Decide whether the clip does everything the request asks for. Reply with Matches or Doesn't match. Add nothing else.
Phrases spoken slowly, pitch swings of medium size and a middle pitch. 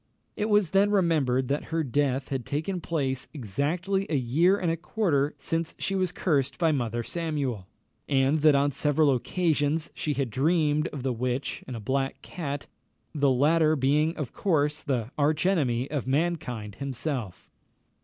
Doesn't match